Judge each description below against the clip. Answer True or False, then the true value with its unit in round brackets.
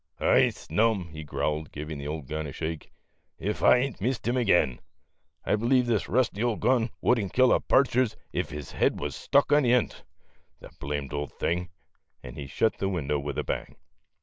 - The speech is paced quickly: True (210 wpm)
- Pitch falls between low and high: False (95 Hz)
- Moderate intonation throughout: False (8.4 semitones)